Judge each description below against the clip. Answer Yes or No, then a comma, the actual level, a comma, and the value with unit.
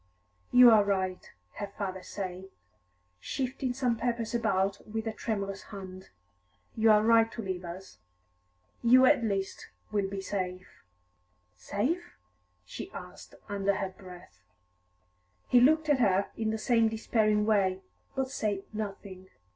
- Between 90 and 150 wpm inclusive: Yes, slow, 135 wpm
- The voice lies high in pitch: Yes, high, 210 Hz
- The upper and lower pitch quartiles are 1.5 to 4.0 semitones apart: Yes, average, 3.2 semitones